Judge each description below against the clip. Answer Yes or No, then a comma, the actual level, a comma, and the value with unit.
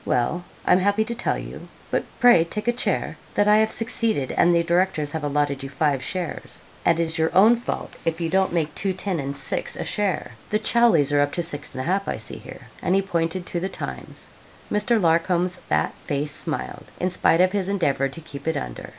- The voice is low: No, medium, 170 Hz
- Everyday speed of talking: No, fast, 220 wpm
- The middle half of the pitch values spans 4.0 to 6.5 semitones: Yes, average, 5.0 semitones